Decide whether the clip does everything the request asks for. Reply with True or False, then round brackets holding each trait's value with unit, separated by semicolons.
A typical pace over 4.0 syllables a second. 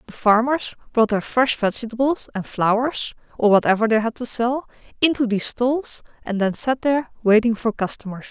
True (5.3 syllables/s)